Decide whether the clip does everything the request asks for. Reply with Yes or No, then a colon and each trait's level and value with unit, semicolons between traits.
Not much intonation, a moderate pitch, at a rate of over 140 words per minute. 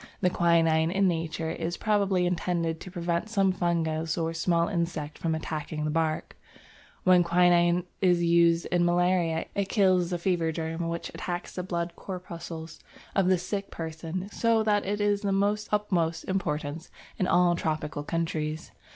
Yes: narrow, 2.2 semitones; medium, 170 Hz; average, 160 wpm